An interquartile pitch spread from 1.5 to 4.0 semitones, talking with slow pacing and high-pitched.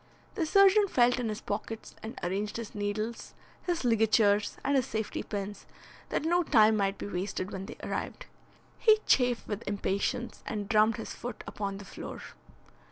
No: average, 3.2 semitones; average, 165 wpm; high, 220 Hz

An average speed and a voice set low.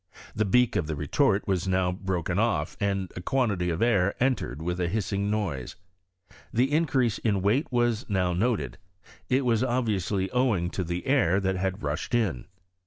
Yes: average, 175 wpm; low, 100 Hz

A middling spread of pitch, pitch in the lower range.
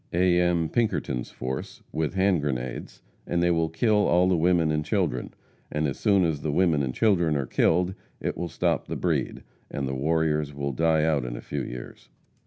Yes: average, 3.7 semitones; very low, 80 Hz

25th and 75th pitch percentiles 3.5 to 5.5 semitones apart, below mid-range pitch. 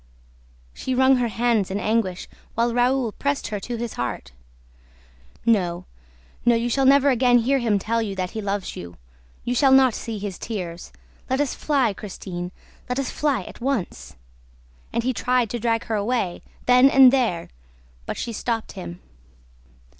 No: average, 4.0 semitones; high, 230 Hz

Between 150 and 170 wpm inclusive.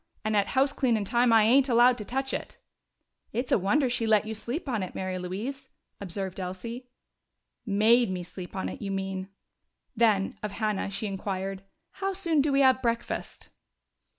No: average, 180 wpm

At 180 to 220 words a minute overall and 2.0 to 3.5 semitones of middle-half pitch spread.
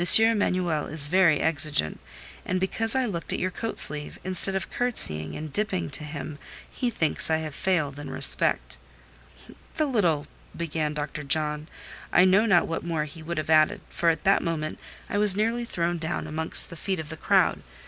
No: average, 185 wpm; average, 4.0 semitones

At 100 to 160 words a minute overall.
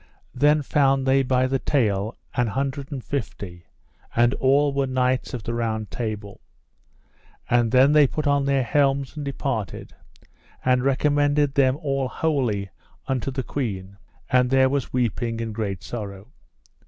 Yes: average, 150 wpm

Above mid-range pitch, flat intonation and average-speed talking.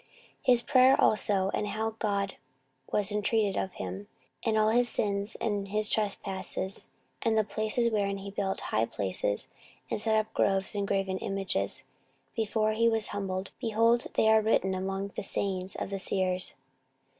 Yes: high, 205 Hz; narrow, 2.2 semitones; average, 165 wpm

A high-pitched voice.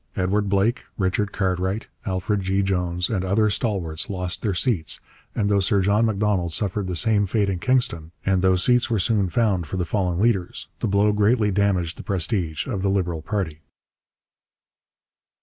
No: very low, 95 Hz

